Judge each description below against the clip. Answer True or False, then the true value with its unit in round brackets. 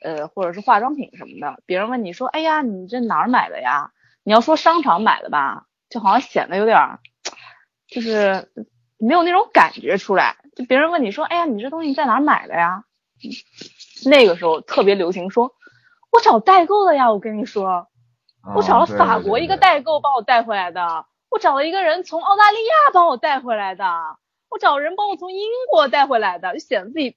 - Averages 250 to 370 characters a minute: True (300 characters per minute)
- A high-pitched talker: True (270 Hz)